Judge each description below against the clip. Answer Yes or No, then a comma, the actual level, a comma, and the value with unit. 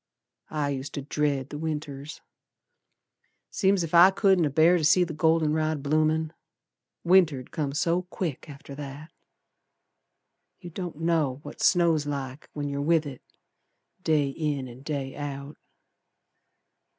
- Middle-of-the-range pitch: Yes, medium, 150 Hz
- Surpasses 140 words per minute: No, slow, 135 wpm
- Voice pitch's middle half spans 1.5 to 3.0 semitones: Yes, average, 2.7 semitones